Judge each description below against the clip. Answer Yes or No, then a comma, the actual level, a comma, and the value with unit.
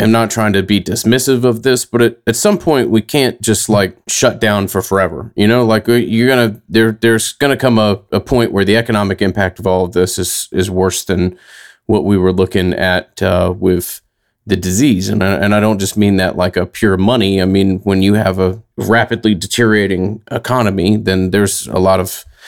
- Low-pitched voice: Yes, low, 105 Hz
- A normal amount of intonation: Yes, average, 3.1 semitones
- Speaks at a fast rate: Yes, fast, 215 wpm